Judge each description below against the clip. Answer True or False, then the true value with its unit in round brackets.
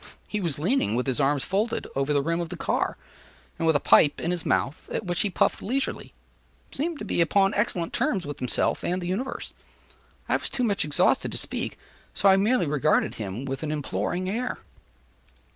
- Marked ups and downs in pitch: True (5.9 semitones)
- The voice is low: False (175 Hz)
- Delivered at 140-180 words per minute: False (200 wpm)